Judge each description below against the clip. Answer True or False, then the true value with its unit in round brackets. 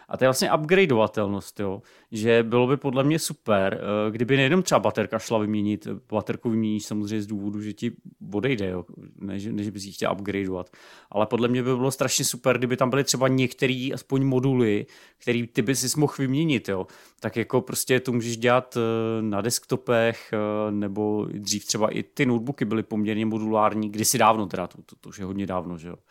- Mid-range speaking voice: False (110 Hz)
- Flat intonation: False (3.5 semitones)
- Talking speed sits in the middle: False (185 wpm)